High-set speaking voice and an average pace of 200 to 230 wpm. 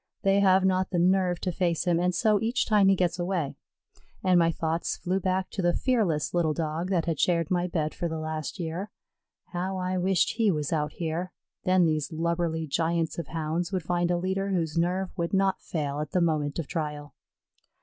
No: medium, 175 Hz; fast, 205 wpm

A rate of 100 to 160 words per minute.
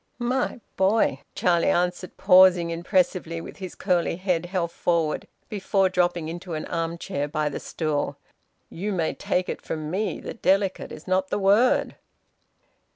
Yes: average, 155 wpm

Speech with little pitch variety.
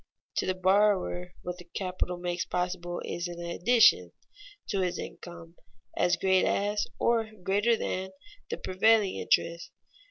Yes: narrow, 2.3 semitones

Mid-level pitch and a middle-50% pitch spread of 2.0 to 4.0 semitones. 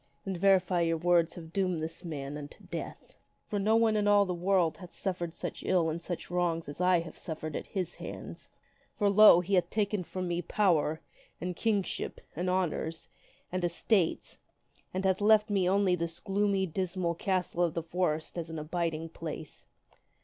Yes: medium, 180 Hz; narrow, 2.6 semitones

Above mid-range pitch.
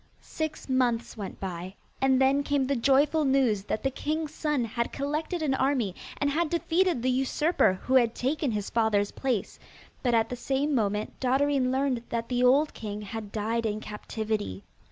Yes: very high, 255 Hz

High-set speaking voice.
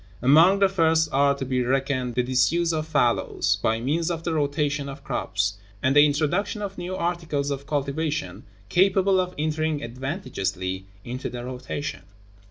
No: medium, 145 Hz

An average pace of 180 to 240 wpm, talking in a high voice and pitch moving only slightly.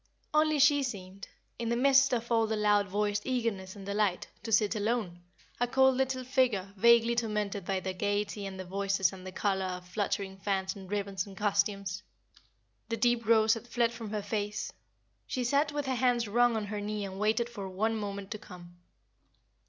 No: average, 190 wpm; high, 210 Hz; average, 3.2 semitones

